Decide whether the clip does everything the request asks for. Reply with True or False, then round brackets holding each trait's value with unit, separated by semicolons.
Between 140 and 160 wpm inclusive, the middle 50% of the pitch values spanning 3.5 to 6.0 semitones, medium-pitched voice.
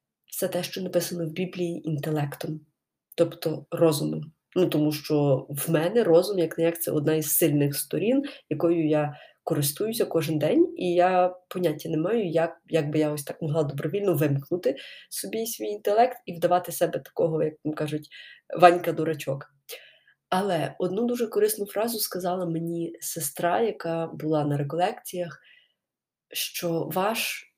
False (150 wpm; 2.8 semitones; 165 Hz)